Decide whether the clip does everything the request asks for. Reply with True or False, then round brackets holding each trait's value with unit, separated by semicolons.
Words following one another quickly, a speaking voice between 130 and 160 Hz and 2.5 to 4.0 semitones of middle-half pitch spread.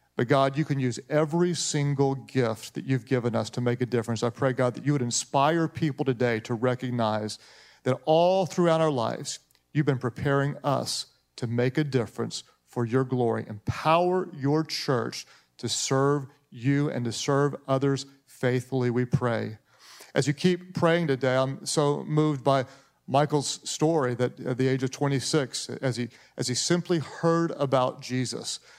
False (170 wpm; 135 Hz; 3.2 semitones)